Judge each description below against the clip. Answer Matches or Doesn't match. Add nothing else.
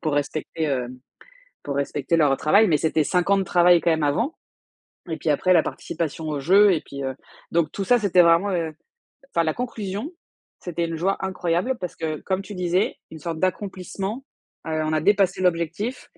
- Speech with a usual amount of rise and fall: Matches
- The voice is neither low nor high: Matches